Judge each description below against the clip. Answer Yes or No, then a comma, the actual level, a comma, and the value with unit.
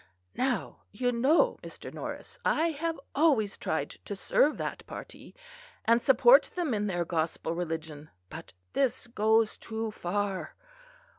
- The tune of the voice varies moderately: No, wide, 7.2 semitones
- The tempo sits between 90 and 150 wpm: Yes, slow, 135 wpm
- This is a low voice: No, high, 220 Hz